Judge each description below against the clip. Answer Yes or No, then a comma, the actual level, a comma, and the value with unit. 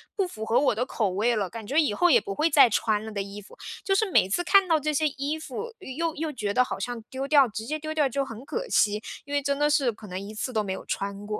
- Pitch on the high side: Yes, very high, 265 Hz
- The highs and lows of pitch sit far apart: Yes, wide, 6.4 semitones